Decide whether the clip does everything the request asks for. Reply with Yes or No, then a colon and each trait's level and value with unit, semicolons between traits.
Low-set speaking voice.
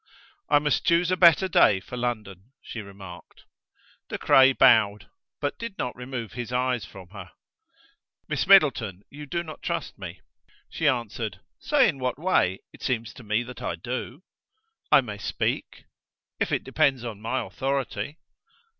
Yes: low, 125 Hz